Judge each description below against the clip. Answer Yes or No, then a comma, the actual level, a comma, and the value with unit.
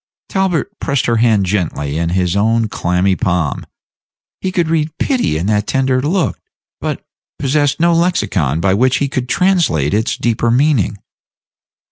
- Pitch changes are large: Yes, wide, 8.7 semitones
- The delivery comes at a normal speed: Yes, average, 150 wpm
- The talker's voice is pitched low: Yes, low, 120 Hz